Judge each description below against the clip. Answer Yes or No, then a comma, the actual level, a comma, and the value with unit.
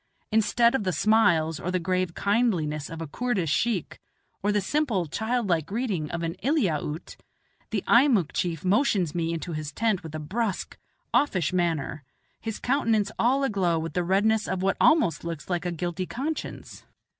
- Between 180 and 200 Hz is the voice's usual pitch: Yes, medium, 185 Hz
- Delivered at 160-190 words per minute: Yes, average, 165 wpm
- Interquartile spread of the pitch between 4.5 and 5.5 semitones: Yes, average, 5.2 semitones